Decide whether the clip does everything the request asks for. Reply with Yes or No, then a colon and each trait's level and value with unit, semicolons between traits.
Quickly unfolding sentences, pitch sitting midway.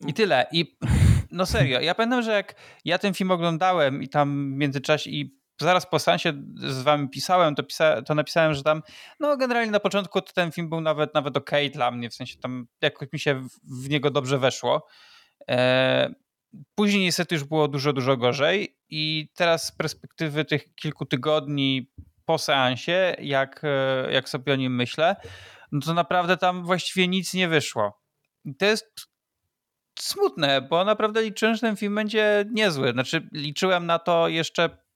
Yes: fast, 175 wpm; medium, 155 Hz